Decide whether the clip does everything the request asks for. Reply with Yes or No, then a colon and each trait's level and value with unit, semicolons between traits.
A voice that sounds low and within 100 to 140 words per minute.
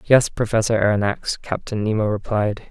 Yes: low, 110 Hz; slow, 135 wpm